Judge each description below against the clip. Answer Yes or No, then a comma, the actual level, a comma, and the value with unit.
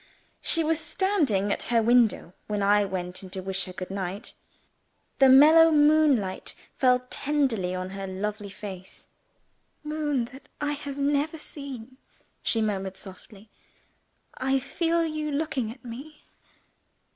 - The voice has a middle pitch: No, high, 245 Hz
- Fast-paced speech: No, slow, 135 wpm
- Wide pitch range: Yes, wide, 7.1 semitones